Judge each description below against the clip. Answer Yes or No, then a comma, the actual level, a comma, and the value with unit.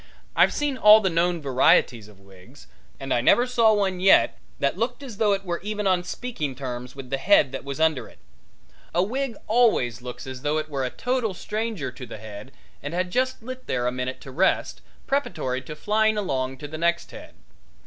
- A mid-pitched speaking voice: Yes, medium, 165 Hz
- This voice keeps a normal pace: No, fast, 210 wpm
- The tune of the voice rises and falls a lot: Yes, wide, 8.5 semitones